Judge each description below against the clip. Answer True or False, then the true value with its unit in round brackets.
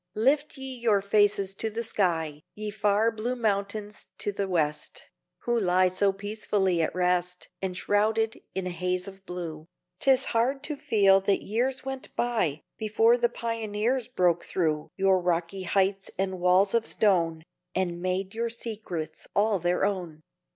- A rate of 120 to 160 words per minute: True (155 wpm)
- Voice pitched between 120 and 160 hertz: False (200 Hz)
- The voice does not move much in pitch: False (3.6 semitones)